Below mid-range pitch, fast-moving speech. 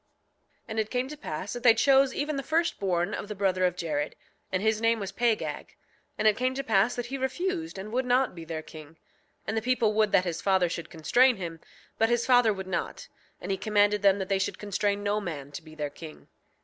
No: high, 210 Hz; fast, 235 wpm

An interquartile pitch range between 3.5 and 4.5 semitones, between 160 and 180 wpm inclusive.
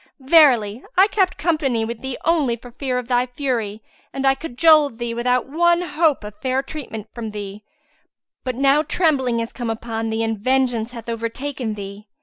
Yes: average, 4.1 semitones; average, 175 wpm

